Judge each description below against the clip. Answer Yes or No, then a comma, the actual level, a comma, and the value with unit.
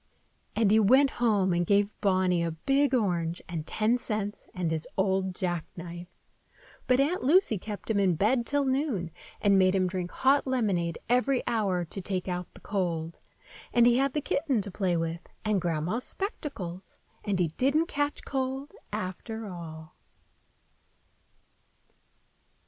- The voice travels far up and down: Yes, wide, 6.1 semitones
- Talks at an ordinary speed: Yes, average, 150 wpm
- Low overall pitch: No, high, 200 Hz